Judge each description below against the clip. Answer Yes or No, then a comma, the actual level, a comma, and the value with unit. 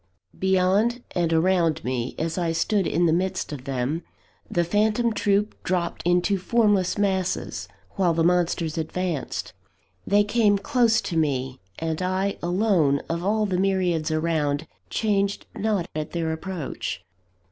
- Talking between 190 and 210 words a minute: No, average, 140 wpm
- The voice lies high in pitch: No, medium, 180 Hz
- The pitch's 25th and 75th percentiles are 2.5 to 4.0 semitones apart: Yes, average, 3.7 semitones